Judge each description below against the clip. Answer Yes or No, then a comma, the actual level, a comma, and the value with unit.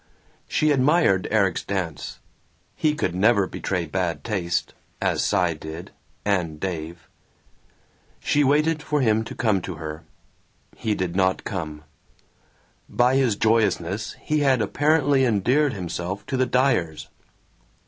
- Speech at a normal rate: No, slow, 130 wpm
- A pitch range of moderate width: No, wide, 7.1 semitones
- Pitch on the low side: Yes, low, 100 Hz